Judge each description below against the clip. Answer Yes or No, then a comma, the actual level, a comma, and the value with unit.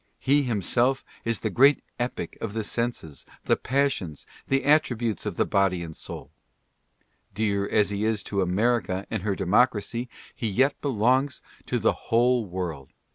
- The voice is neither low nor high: No, low, 110 Hz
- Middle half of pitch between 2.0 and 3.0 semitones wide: No, average, 4.3 semitones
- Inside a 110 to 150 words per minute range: No, average, 160 wpm